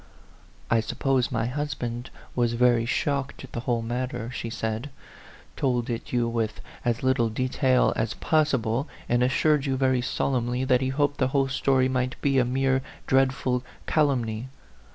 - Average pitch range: No, narrow, 2.1 semitones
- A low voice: Yes, low, 125 Hz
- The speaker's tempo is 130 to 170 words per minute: Yes, average, 165 wpm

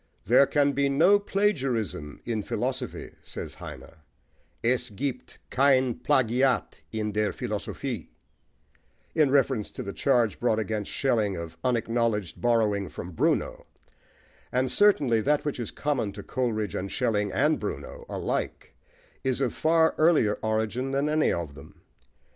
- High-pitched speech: No, low, 120 Hz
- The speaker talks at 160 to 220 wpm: No, slow, 135 wpm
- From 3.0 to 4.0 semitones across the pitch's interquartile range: No, average, 4.5 semitones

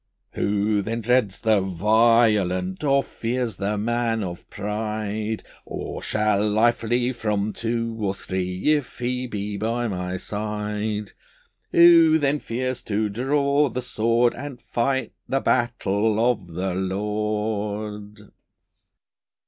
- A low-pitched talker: Yes, low, 110 Hz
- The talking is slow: Yes, slow, 120 wpm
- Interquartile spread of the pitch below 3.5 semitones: Yes, average, 2.8 semitones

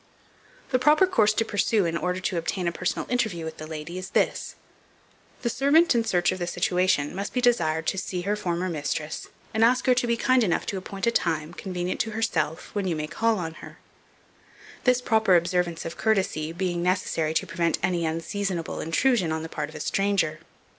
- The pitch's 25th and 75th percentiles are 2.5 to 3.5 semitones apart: No, average, 4.9 semitones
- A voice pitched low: No, medium, 185 Hz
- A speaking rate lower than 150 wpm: No, average, 200 wpm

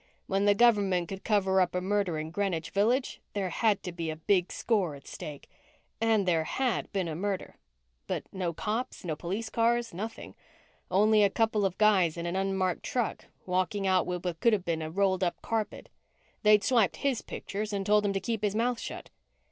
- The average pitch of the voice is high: Yes, high, 195 Hz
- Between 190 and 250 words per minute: Yes, average, 200 wpm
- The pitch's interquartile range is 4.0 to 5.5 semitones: No, average, 3.1 semitones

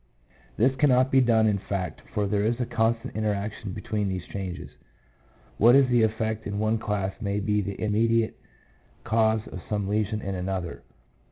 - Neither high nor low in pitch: No, low, 110 Hz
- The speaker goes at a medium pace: Yes, average, 170 wpm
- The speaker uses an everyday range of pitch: No, narrow, 2.2 semitones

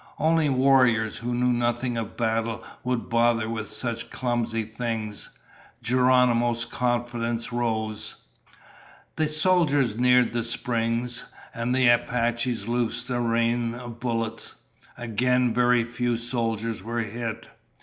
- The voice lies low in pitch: Yes, low, 120 Hz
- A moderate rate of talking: No, slow, 120 wpm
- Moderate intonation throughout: No, narrow, 1.4 semitones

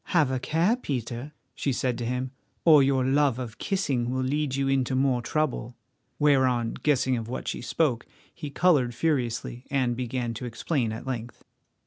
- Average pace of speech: Yes, average, 170 wpm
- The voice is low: Yes, low, 130 Hz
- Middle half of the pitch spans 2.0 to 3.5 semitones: Yes, average, 3.0 semitones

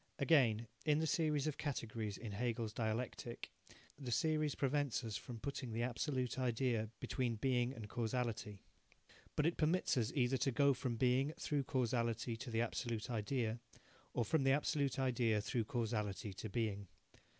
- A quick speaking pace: No, average, 160 wpm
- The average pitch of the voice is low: Yes, low, 120 Hz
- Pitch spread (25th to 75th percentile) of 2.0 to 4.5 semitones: Yes, average, 3.4 semitones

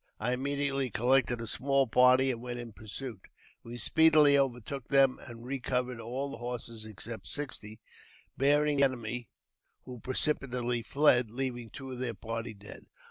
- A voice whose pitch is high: No, low, 125 Hz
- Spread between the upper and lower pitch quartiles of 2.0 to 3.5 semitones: Yes, average, 2.7 semitones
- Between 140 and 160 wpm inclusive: Yes, average, 155 wpm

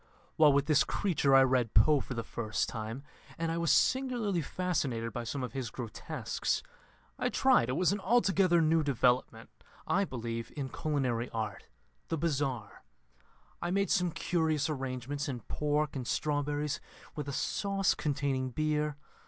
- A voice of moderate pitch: Yes, medium, 145 Hz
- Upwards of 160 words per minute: No, average, 155 wpm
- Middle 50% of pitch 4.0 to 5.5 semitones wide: Yes, average, 4.6 semitones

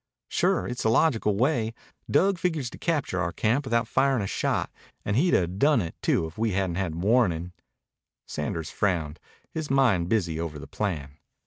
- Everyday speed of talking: Yes, average, 180 wpm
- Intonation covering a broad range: Yes, wide, 7.3 semitones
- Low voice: Yes, low, 105 Hz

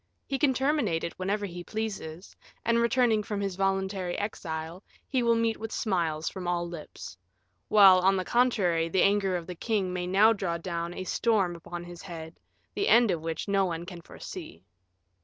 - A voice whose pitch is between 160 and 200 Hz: Yes, high, 190 Hz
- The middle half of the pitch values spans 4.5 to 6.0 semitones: No, average, 3.9 semitones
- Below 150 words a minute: No, average, 185 wpm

